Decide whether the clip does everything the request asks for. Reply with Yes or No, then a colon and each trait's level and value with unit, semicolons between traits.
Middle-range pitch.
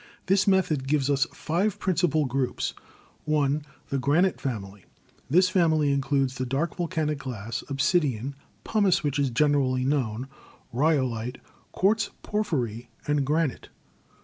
Yes: medium, 145 Hz